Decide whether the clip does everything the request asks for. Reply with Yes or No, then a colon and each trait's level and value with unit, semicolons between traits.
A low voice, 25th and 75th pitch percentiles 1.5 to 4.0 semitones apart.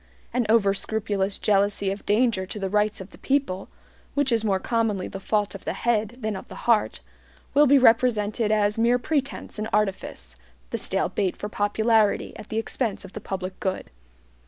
No: high, 210 Hz; average, 2.7 semitones